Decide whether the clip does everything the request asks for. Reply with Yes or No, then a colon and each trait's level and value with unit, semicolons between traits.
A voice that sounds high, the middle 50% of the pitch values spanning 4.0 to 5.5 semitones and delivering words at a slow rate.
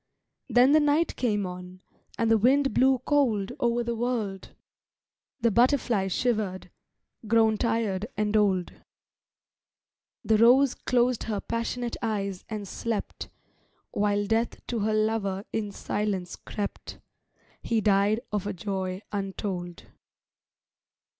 No: high, 215 Hz; average, 3.1 semitones; slow, 120 wpm